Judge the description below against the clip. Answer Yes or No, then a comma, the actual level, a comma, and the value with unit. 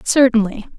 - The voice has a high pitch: Yes, high, 225 Hz